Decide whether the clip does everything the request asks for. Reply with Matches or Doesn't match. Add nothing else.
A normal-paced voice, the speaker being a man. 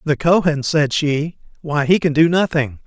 Matches